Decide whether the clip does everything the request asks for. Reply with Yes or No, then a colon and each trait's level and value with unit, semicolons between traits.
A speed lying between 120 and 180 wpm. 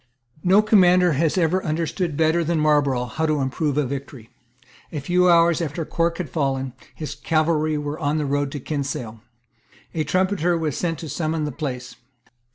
Yes: average, 170 wpm